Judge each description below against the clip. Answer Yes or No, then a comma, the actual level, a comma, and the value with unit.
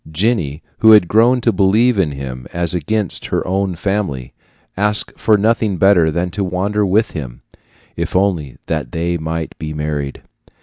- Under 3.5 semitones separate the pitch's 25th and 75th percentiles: No, average, 5.1 semitones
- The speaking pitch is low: Yes, very low, 90 Hz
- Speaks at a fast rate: No, average, 160 wpm